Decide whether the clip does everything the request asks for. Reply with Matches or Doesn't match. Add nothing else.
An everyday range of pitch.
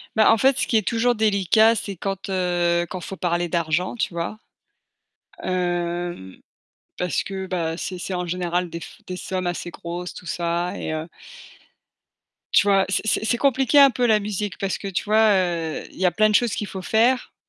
Matches